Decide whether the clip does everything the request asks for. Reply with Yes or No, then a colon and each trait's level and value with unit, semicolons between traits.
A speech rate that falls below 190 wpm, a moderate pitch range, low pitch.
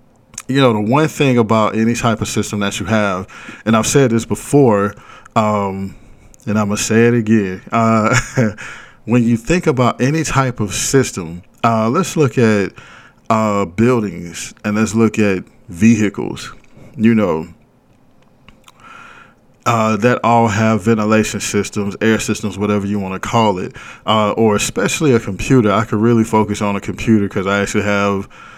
No: average, 165 wpm; narrow, 2.3 semitones; low, 110 Hz